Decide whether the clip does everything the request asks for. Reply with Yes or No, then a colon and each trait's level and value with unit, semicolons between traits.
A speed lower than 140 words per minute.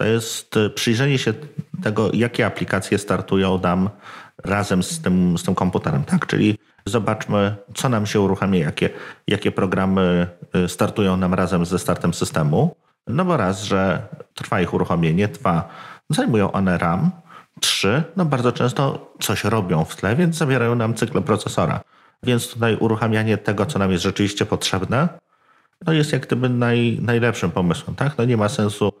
No: average, 155 wpm